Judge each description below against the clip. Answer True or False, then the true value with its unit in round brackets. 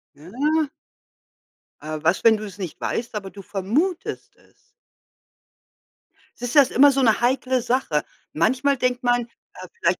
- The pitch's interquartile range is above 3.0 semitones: True (5.1 semitones)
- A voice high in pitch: True (240 Hz)